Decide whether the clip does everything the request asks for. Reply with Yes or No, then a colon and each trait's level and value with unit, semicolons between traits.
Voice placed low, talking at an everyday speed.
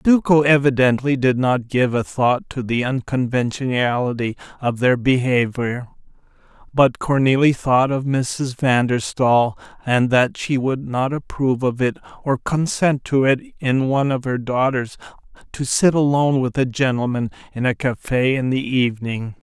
Yes: low, 130 Hz; average, 155 wpm